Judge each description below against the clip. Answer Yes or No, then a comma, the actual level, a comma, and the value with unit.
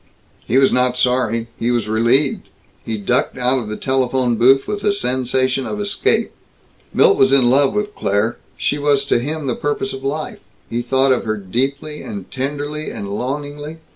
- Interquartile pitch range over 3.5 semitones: No, average, 3.2 semitones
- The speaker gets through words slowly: No, average, 180 wpm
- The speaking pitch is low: Yes, low, 130 Hz